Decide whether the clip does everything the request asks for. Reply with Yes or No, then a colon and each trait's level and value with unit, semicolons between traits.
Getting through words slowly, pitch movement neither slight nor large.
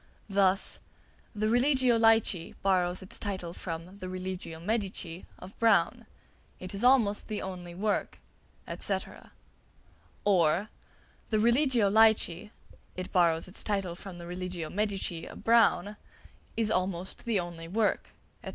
Yes: slow, 130 wpm; average, 3.4 semitones